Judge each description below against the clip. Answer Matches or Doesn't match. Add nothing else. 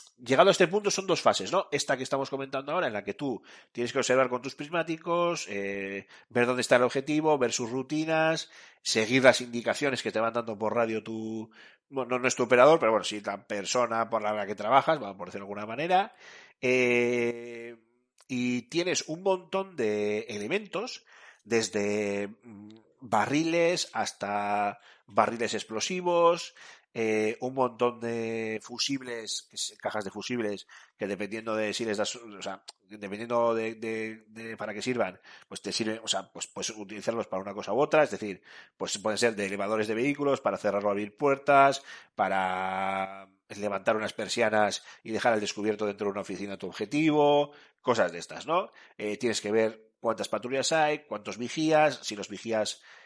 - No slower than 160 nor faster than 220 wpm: Matches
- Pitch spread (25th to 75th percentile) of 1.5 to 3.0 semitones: Doesn't match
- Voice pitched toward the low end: Matches